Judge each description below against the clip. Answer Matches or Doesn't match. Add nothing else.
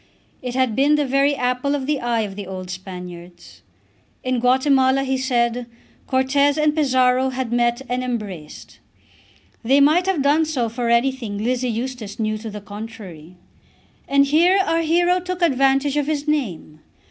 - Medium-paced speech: Matches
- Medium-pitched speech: Doesn't match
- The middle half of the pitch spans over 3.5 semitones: Matches